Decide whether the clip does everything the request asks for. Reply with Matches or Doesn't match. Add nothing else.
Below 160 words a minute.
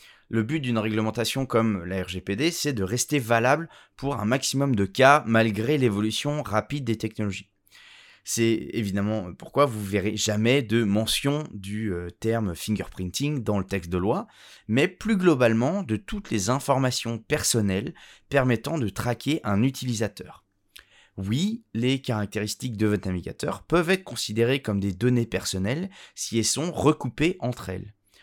Matches